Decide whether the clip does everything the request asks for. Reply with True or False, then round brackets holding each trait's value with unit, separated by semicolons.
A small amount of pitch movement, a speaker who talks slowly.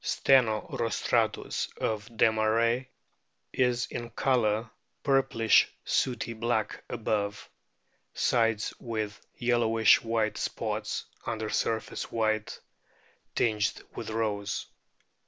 True (1.5 semitones; 85 wpm)